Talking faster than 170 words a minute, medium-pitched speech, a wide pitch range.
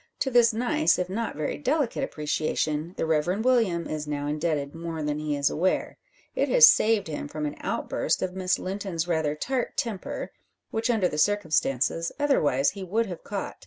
Yes: average, 180 wpm; medium, 180 Hz; wide, 6.7 semitones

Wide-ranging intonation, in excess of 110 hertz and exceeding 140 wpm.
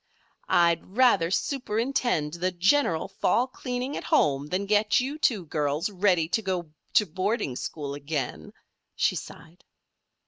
No: wide, 6.3 semitones; medium, 185 Hz; slow, 135 wpm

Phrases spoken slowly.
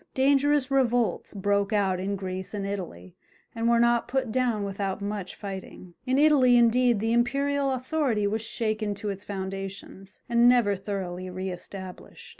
No: average, 155 wpm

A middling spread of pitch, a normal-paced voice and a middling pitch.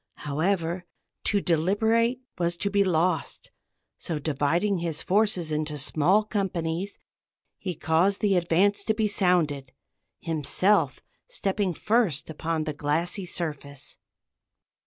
No: average, 4.2 semitones; slow, 115 wpm; medium, 175 Hz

